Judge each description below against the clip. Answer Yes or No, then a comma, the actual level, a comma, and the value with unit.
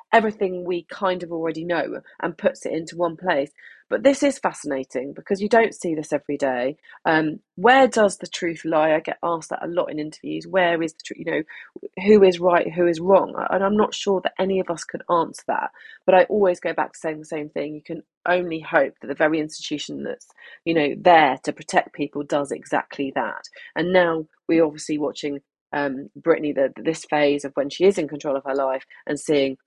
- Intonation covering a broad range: No, average, 3.7 semitones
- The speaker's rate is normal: No, fast, 220 wpm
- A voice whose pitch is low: No, medium, 165 Hz